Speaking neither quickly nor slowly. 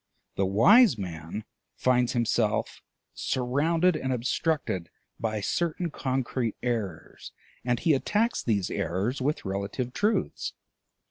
No: slow, 110 wpm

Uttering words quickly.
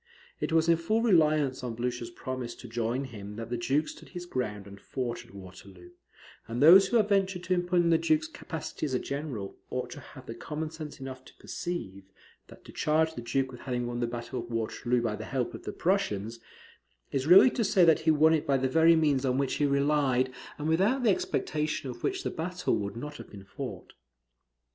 Yes: fast, 220 wpm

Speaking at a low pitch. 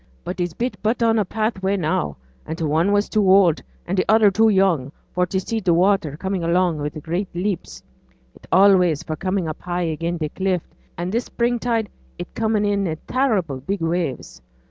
No: medium, 185 Hz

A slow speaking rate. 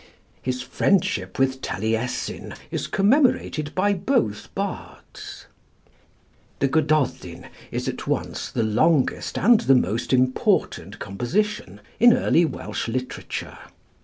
Yes: slow, 105 wpm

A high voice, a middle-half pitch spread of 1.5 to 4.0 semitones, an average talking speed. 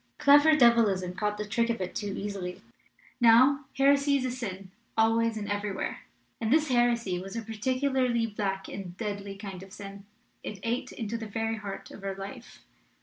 Yes: high, 220 Hz; average, 3.5 semitones; average, 175 wpm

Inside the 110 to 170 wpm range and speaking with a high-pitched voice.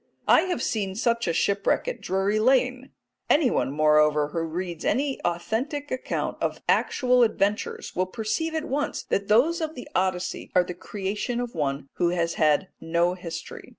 Yes: average, 165 wpm; high, 200 Hz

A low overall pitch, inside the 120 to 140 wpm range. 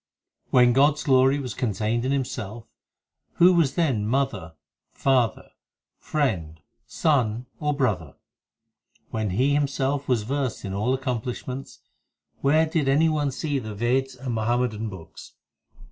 Yes: low, 130 Hz; slow, 135 wpm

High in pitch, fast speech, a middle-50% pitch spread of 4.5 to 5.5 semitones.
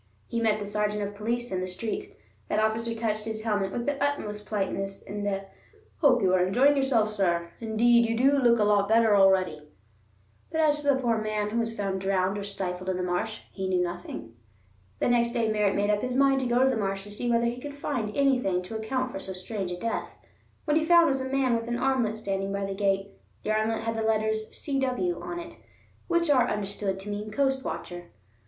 No: high, 220 Hz; fast, 225 wpm; average, 4.1 semitones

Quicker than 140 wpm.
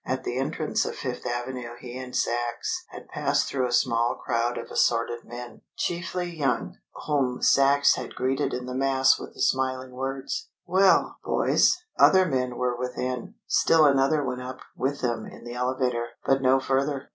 Yes: average, 170 wpm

